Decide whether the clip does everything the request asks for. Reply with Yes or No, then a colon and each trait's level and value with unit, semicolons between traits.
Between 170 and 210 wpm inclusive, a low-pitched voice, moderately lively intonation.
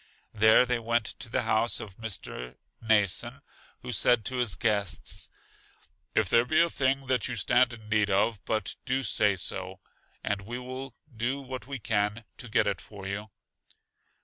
Yes: average, 175 wpm; low, 110 Hz; average, 3.3 semitones